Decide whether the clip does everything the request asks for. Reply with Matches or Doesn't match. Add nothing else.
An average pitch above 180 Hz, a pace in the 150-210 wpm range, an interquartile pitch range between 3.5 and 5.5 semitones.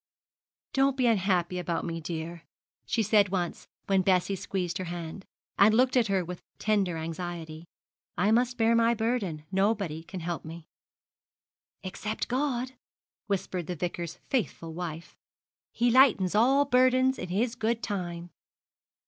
Doesn't match